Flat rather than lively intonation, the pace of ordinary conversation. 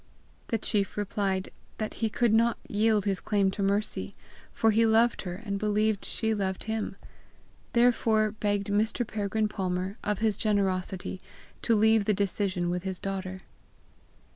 Yes: narrow, 2.2 semitones; average, 150 wpm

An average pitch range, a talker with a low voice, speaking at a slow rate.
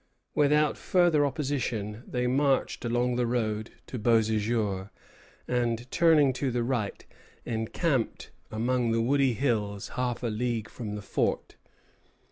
Yes: average, 3.3 semitones; low, 120 Hz; slow, 125 wpm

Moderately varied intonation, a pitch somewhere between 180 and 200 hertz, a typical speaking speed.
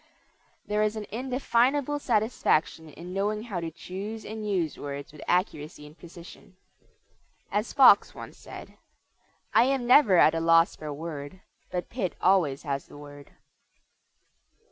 No: wide, 5.7 semitones; medium, 185 Hz; average, 145 wpm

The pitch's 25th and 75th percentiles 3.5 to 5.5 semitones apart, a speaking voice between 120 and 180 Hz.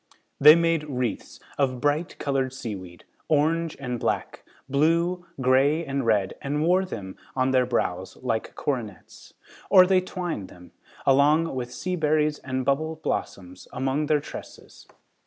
Yes: average, 4.1 semitones; medium, 140 Hz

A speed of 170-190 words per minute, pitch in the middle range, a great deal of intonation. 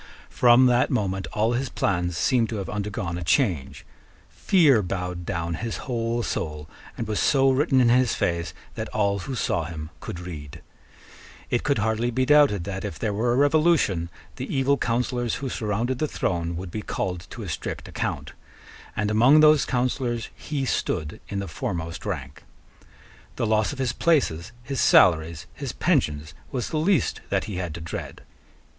No: average, 175 wpm; low, 110 Hz; wide, 6.6 semitones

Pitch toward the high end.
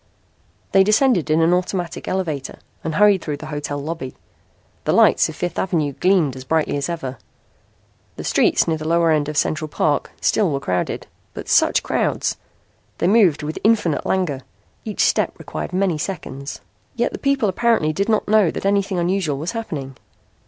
No: medium, 165 Hz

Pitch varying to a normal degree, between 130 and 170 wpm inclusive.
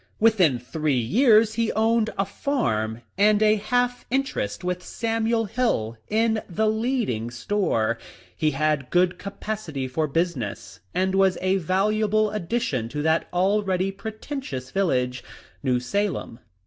No: wide, 7.5 semitones; slow, 135 wpm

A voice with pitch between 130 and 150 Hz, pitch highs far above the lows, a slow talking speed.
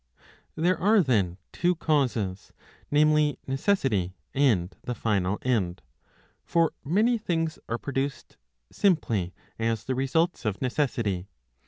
Yes: low, 135 Hz; wide, 7.5 semitones; slow, 120 wpm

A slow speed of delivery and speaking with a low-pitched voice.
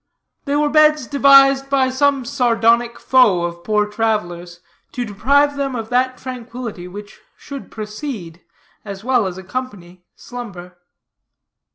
No: slow, 130 wpm; high, 235 Hz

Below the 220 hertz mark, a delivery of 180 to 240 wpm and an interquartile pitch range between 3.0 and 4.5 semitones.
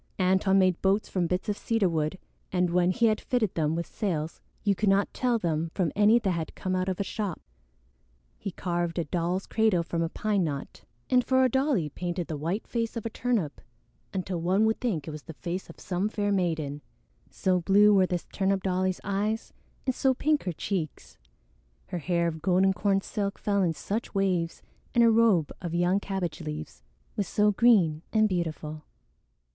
Yes: medium, 185 Hz; average, 195 wpm; average, 3.6 semitones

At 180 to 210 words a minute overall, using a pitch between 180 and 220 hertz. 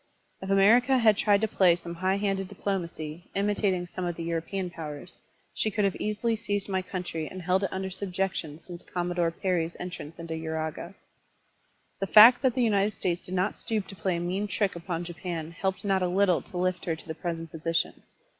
Yes: average, 200 wpm; medium, 185 Hz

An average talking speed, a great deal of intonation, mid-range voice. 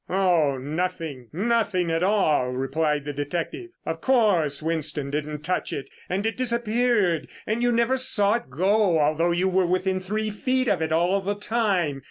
Yes: average, 170 wpm; wide, 5.9 semitones; medium, 180 Hz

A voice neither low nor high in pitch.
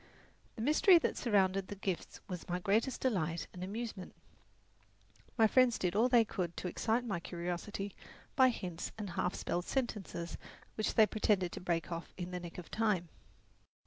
No: high, 195 Hz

